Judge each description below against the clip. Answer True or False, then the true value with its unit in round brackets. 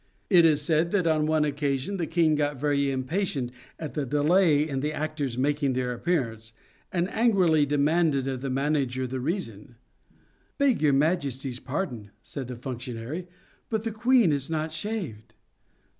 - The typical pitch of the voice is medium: True (145 Hz)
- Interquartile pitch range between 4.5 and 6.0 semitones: False (4.1 semitones)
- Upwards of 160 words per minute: True (170 wpm)